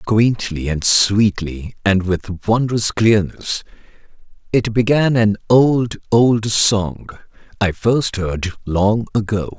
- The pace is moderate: No, slow, 115 wpm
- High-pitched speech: No, low, 105 Hz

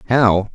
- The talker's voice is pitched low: Yes, low, 110 Hz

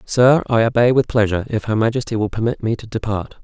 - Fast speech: Yes, fast, 225 wpm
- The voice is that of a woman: No, male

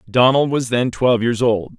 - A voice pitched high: No, low, 120 Hz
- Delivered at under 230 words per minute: Yes, average, 200 wpm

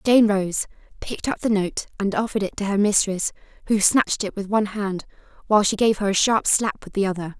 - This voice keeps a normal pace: No, fast, 225 wpm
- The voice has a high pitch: Yes, high, 205 Hz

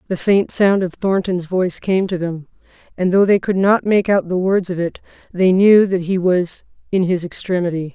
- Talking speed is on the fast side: Yes, fast, 210 wpm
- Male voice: No, female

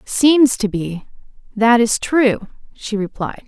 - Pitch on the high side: Yes, high, 230 Hz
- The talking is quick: No, slow, 120 wpm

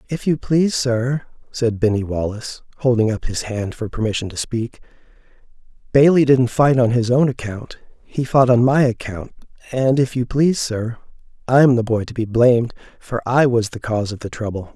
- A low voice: Yes, low, 120 Hz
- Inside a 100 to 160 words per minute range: No, average, 190 wpm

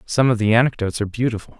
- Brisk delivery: Yes, fast, 225 wpm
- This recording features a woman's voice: No, male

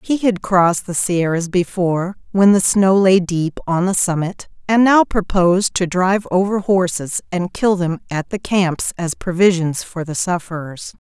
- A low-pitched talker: No, medium, 180 Hz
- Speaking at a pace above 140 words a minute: Yes, average, 175 wpm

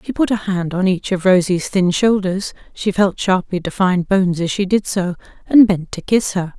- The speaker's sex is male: No, female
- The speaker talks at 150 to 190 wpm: No, average, 200 wpm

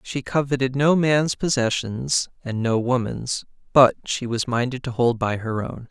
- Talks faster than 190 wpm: No, average, 160 wpm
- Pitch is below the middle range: Yes, low, 125 Hz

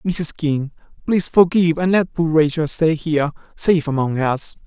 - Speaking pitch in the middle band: Yes, medium, 160 Hz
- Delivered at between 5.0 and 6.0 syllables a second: Yes, 5.1 syllables/s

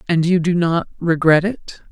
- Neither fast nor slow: Yes, average, 190 wpm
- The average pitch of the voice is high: No, medium, 170 Hz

